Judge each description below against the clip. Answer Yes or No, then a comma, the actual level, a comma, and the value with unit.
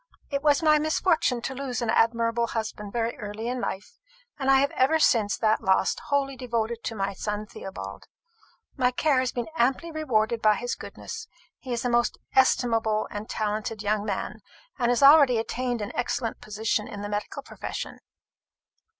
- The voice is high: Yes, high, 235 Hz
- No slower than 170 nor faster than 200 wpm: Yes, average, 175 wpm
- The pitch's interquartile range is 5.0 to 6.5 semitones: No, average, 3.4 semitones